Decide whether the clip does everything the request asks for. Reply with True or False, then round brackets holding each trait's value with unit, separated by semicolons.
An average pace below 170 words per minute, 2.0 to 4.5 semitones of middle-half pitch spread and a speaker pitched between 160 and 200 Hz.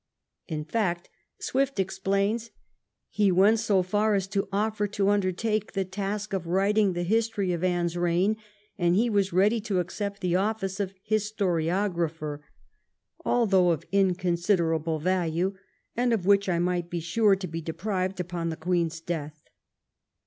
True (150 wpm; 3.0 semitones; 190 Hz)